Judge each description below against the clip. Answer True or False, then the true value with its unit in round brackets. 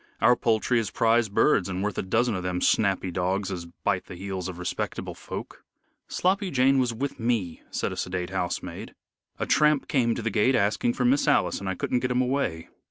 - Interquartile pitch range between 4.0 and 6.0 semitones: True (5.1 semitones)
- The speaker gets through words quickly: True (210 wpm)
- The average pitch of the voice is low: True (110 Hz)